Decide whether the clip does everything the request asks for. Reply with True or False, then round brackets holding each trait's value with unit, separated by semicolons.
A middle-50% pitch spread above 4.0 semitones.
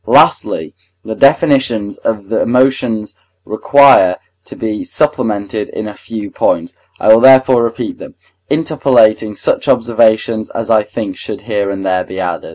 False (3.3 semitones)